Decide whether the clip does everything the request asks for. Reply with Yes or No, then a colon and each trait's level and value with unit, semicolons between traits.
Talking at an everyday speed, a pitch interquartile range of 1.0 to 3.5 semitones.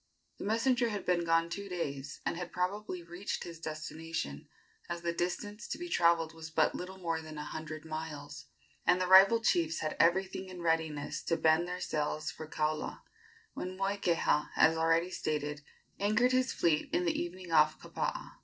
Yes: average, 175 wpm; average, 2.8 semitones